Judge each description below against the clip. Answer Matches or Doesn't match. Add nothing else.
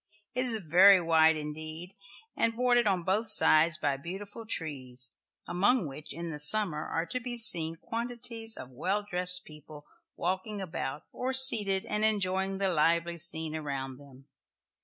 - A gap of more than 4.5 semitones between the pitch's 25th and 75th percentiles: Matches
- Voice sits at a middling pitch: Matches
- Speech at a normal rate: Matches